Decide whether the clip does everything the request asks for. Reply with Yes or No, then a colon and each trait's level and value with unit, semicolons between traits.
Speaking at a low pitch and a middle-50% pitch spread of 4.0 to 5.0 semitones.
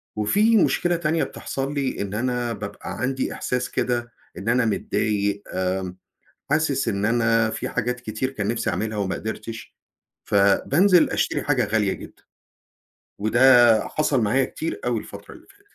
Yes: low, 120 Hz; average, 4.4 semitones